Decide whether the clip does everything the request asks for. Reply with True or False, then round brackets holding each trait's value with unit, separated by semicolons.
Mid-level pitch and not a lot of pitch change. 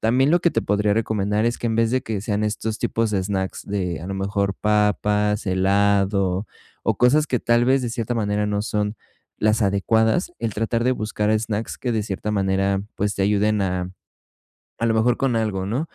False (105 Hz; 2.3 semitones)